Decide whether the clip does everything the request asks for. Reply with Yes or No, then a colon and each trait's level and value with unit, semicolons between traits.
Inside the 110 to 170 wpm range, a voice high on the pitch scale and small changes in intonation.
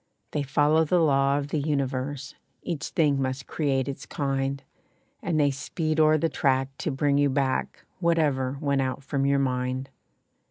No: average, 165 wpm; medium, 140 Hz; narrow, 1.9 semitones